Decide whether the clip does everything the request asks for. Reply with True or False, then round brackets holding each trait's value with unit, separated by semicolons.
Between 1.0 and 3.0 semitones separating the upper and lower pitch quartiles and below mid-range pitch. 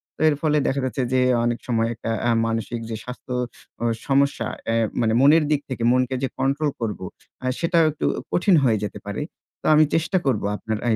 False (4.2 semitones; 130 Hz)